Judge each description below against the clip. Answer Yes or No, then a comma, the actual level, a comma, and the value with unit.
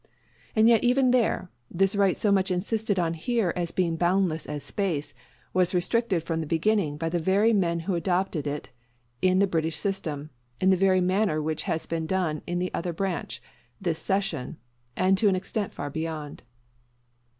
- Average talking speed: Yes, average, 180 wpm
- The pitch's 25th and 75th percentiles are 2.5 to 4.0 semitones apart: Yes, average, 3.2 semitones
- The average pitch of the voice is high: No, medium, 180 Hz